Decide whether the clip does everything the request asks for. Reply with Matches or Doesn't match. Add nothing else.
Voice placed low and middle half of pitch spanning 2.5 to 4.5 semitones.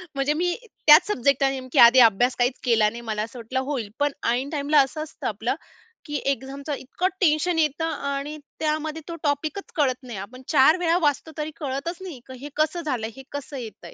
Doesn't match